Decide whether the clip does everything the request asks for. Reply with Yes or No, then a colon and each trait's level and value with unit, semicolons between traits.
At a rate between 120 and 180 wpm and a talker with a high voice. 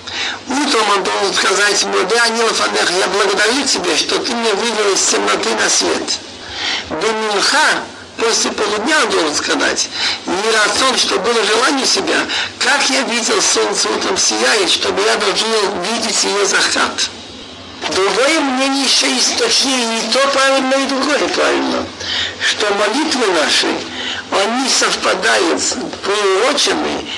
Yes: average, 140 wpm; very high, 255 Hz